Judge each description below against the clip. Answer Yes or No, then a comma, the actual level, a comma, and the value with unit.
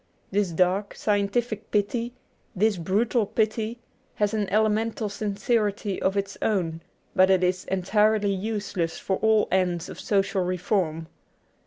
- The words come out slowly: Yes, slow, 130 wpm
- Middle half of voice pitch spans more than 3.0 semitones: No, narrow, 2.5 semitones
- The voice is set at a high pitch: Yes, high, 200 Hz